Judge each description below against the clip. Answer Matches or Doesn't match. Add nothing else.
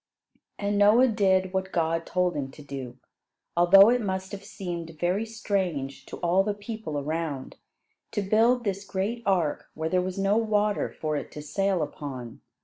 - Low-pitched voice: Doesn't match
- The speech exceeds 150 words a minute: Matches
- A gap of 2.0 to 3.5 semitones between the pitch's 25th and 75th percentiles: Doesn't match